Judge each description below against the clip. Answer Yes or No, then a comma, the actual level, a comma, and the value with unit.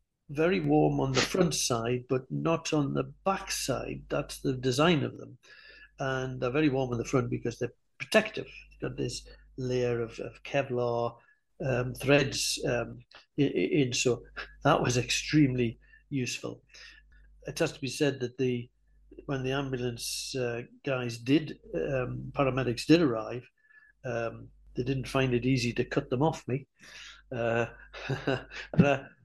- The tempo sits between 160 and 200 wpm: No, average, 150 wpm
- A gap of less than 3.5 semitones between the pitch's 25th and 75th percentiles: Yes, average, 2.9 semitones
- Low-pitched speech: Yes, low, 130 Hz